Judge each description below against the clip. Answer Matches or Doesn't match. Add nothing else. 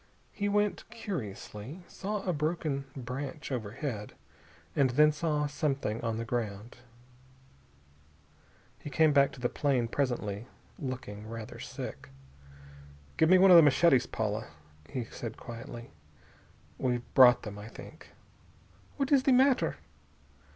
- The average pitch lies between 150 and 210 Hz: Doesn't match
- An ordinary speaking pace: Doesn't match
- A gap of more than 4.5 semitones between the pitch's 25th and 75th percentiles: Matches